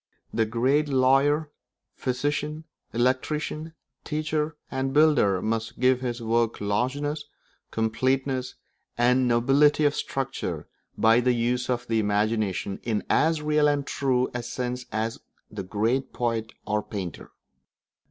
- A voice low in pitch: Yes, low, 125 Hz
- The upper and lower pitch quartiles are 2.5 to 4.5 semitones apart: Yes, average, 4.1 semitones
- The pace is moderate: No, slow, 125 wpm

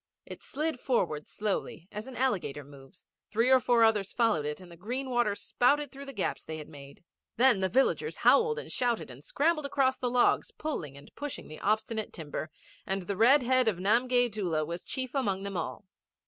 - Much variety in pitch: Yes, wide, 6.7 semitones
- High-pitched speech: Yes, high, 220 Hz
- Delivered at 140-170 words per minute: No, average, 200 wpm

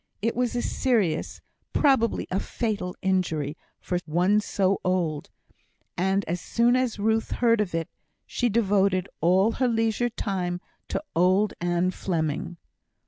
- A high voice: Yes, high, 195 Hz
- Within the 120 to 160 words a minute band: Yes, average, 140 wpm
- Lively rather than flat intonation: No, average, 4.3 semitones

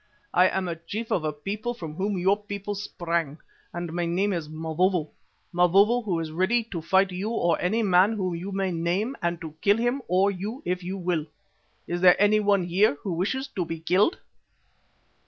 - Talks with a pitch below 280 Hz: Yes, medium, 185 Hz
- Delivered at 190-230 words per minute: Yes, average, 195 wpm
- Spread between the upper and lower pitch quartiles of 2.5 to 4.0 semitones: Yes, average, 3.0 semitones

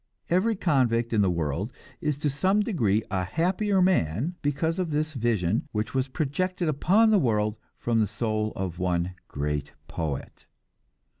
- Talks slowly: No, average, 155 wpm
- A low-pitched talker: Yes, low, 120 Hz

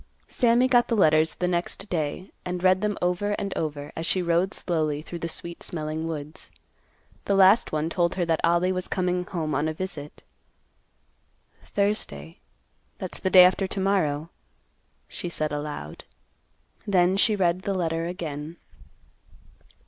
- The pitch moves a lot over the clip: No, average, 3.3 semitones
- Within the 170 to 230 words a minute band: No, average, 155 wpm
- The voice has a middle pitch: Yes, medium, 175 Hz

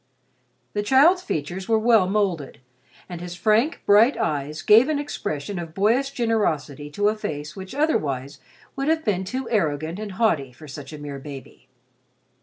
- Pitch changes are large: Yes, wide, 7.4 semitones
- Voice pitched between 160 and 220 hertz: Yes, high, 190 Hz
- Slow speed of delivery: No, average, 165 wpm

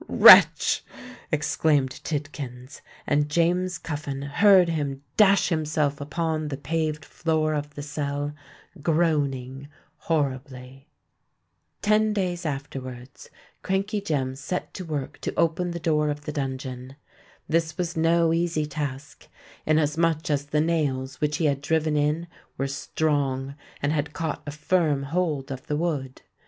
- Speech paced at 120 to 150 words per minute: Yes, slow, 135 wpm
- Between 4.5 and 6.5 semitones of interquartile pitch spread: No, average, 2.8 semitones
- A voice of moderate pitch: Yes, medium, 150 Hz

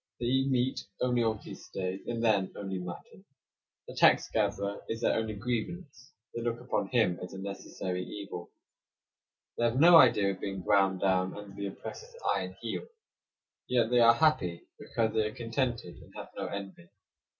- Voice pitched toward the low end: Yes, low, 110 Hz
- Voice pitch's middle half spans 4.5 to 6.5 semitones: No, average, 4.0 semitones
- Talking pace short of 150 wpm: No, average, 175 wpm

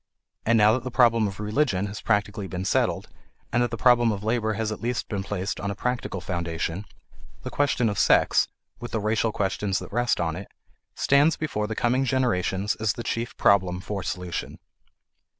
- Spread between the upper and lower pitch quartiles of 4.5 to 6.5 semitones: No, average, 3.5 semitones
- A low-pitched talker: Yes, low, 105 Hz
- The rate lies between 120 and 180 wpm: No, average, 190 wpm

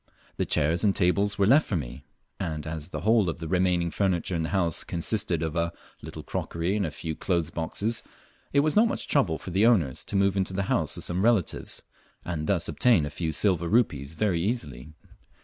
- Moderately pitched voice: No, very low, 90 Hz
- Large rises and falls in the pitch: No, average, 3.8 semitones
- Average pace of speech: No, fast, 210 wpm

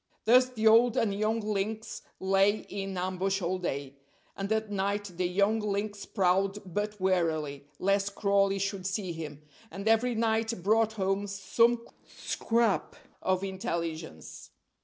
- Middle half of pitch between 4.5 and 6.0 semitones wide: No, narrow, 2.6 semitones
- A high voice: Yes, high, 195 Hz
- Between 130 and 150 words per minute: Yes, average, 140 wpm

